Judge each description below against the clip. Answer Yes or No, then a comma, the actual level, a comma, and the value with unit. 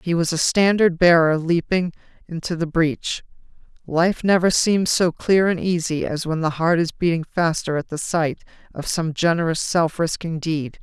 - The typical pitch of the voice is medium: Yes, medium, 170 Hz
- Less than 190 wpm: Yes, average, 175 wpm